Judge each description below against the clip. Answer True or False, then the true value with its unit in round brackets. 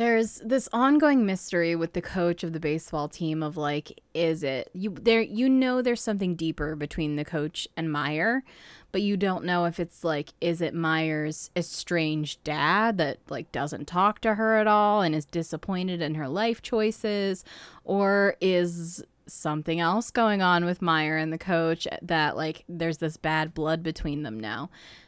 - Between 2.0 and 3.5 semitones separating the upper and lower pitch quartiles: False (4.2 semitones)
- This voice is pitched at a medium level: True (170 Hz)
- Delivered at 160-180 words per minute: True (175 wpm)